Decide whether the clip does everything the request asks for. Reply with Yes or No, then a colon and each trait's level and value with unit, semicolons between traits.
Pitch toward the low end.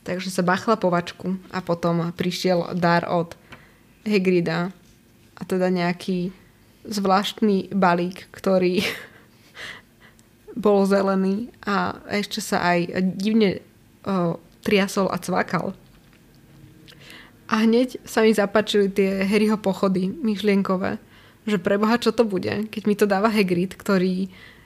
No: high, 195 Hz